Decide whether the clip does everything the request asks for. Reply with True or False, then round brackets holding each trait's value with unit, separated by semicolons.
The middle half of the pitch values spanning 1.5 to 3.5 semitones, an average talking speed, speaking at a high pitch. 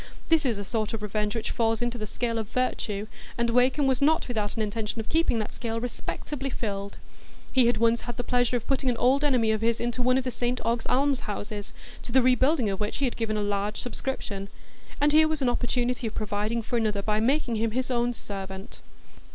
False (2.9 semitones; 225 wpm; 235 Hz)